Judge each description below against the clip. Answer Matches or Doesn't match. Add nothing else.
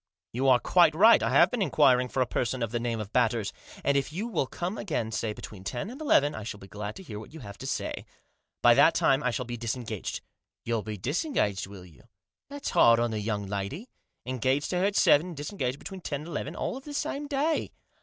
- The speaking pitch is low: Matches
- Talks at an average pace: Doesn't match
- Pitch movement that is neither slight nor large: Doesn't match